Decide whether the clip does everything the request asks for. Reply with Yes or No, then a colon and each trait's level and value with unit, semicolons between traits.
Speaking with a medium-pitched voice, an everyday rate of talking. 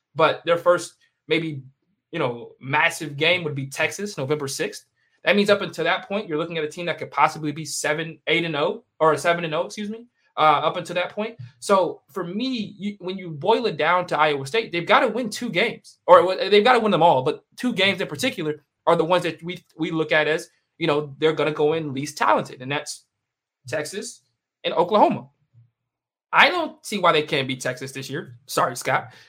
No: medium, 160 Hz; fast, 220 wpm